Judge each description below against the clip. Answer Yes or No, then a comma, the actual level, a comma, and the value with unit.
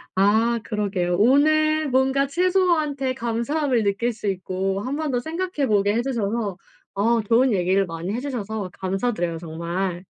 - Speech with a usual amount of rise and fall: No, wide, 5.9 semitones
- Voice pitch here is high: Yes, high, 230 Hz